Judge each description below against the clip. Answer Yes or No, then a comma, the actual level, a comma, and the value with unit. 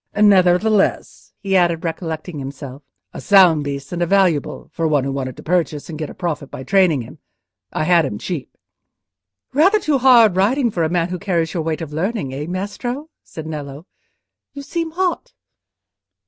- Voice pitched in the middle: Yes, medium, 175 Hz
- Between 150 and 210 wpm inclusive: Yes, average, 175 wpm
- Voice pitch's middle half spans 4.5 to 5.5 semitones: Yes, average, 5.0 semitones